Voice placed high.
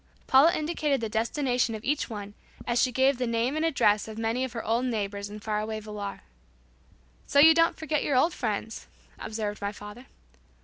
Yes: high, 230 Hz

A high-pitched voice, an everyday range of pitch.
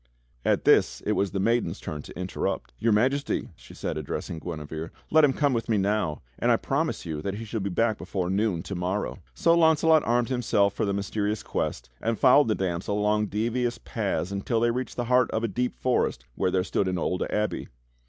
No: low, 105 Hz; average, 4.1 semitones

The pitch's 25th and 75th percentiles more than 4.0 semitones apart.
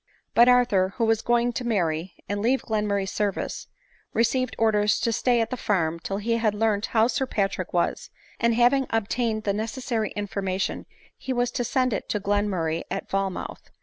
No: average, 3.2 semitones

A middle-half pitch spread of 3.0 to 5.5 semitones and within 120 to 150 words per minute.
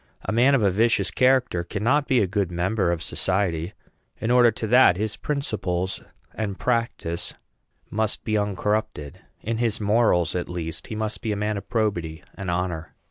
No: average, 4.2 semitones; average, 175 wpm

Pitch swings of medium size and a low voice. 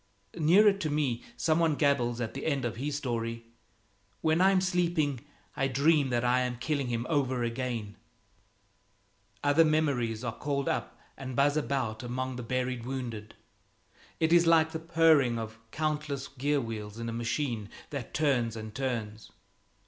Yes: average, 4.4 semitones; low, 130 Hz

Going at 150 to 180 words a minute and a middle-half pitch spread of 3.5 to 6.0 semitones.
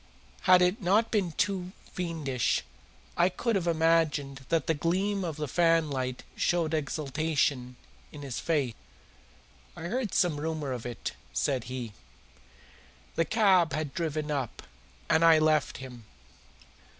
No: slow, 135 wpm; average, 4.1 semitones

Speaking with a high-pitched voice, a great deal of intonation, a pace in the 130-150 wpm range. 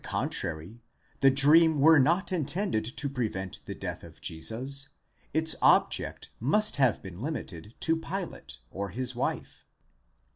No: low, 135 Hz; wide, 6.6 semitones; slow, 135 wpm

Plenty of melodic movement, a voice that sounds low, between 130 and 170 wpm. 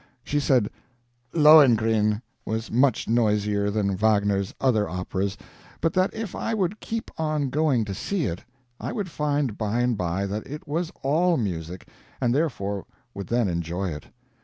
Yes: wide, 7.0 semitones; low, 115 Hz; average, 155 wpm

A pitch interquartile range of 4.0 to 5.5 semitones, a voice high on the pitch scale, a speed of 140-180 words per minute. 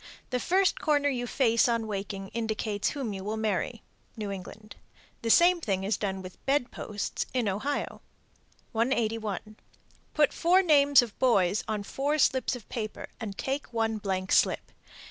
Yes: average, 4.7 semitones; high, 225 Hz; average, 165 wpm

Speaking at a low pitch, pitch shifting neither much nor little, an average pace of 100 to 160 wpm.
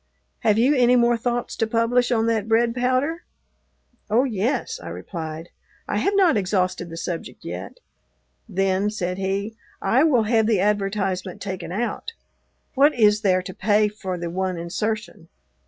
No: high, 210 Hz; average, 4.3 semitones; average, 155 wpm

